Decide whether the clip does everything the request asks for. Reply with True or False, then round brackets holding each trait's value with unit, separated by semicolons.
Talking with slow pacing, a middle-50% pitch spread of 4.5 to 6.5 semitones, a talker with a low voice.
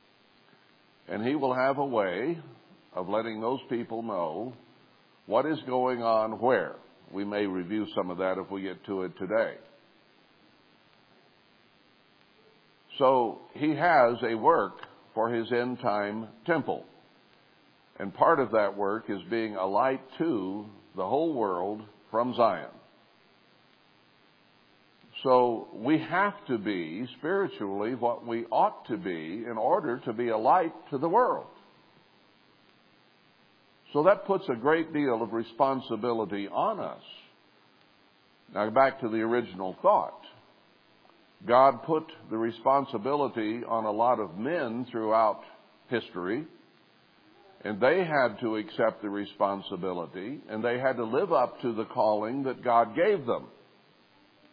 False (130 wpm; 3.4 semitones; 110 Hz)